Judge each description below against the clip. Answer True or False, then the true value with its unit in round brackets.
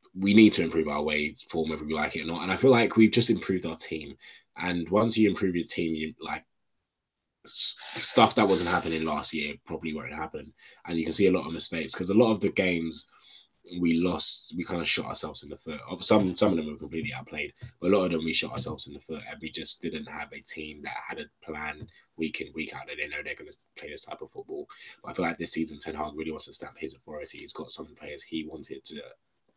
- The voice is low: True (85 Hz)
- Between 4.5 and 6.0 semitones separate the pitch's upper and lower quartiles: True (4.8 semitones)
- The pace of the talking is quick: True (260 wpm)